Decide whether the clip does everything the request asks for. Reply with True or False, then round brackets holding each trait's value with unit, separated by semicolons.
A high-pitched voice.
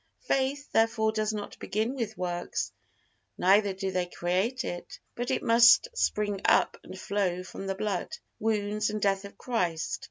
True (210 Hz)